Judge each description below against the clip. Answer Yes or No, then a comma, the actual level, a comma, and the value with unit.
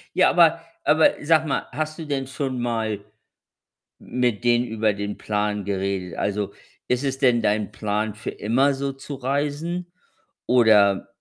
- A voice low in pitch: Yes, low, 120 Hz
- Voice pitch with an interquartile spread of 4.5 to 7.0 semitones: Yes, average, 5.2 semitones